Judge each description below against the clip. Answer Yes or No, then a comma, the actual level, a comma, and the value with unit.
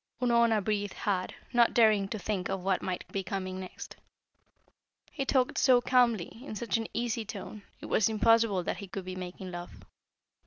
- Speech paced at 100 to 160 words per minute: No, average, 180 wpm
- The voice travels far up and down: No, average, 3.7 semitones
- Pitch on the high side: Yes, high, 210 Hz